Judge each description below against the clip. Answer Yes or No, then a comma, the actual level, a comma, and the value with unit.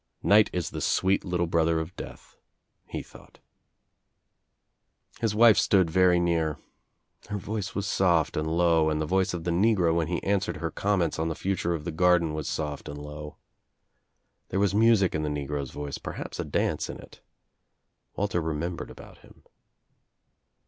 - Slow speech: No, average, 160 wpm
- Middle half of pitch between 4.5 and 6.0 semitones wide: No, average, 3.5 semitones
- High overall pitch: No, very low, 85 Hz